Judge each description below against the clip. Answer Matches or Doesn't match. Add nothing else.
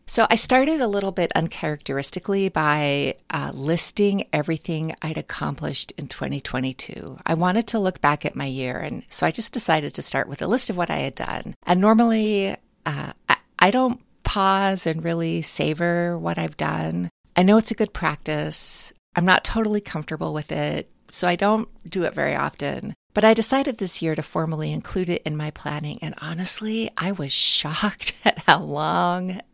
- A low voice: Doesn't match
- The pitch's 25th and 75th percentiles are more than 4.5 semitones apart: Matches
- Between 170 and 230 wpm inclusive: Matches